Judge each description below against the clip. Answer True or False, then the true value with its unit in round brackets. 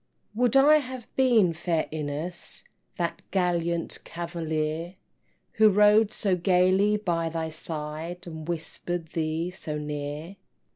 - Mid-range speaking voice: True (170 Hz)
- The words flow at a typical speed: False (115 wpm)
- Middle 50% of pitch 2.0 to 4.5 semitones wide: True (3.7 semitones)